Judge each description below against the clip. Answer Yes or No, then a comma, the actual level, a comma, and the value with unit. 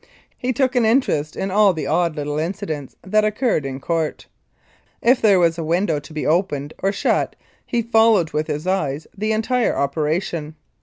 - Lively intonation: Yes, wide, 5.9 semitones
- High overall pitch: No, medium, 175 Hz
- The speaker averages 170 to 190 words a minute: Yes, average, 175 wpm